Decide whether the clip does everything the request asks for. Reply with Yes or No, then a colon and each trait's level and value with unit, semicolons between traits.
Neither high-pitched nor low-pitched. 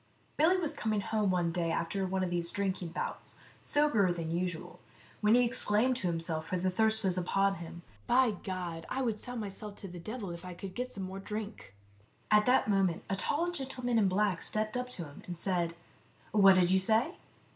No: high, 195 Hz